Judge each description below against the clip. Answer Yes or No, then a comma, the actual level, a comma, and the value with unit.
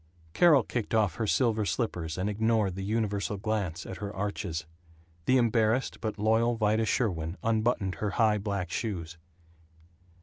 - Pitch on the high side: No, low, 105 Hz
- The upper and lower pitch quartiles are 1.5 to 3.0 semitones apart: Yes, average, 2.7 semitones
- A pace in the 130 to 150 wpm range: Yes, average, 145 wpm